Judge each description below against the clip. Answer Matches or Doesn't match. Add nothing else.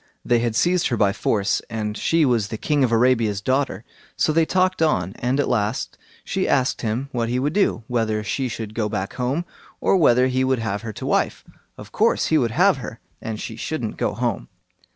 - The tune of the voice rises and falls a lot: Doesn't match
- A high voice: Doesn't match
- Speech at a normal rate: Doesn't match